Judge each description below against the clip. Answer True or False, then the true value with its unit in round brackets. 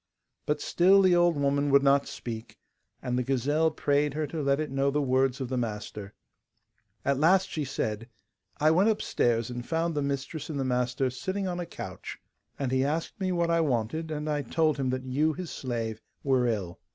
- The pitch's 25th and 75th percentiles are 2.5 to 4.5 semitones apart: True (4.0 semitones)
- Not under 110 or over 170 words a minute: False (200 wpm)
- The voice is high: False (140 Hz)